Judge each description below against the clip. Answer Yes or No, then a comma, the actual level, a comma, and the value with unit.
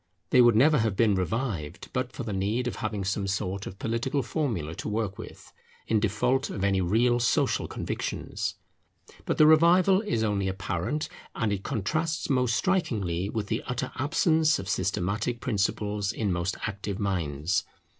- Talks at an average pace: Yes, average, 165 wpm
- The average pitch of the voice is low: Yes, low, 110 Hz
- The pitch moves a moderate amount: Yes, average, 4.6 semitones